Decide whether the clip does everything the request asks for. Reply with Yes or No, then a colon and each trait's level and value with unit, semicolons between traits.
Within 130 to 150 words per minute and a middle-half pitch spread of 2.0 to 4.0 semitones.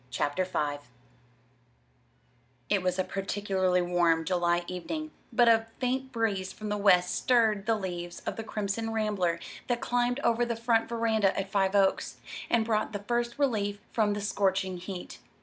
No: average, 160 wpm; average, 3.7 semitones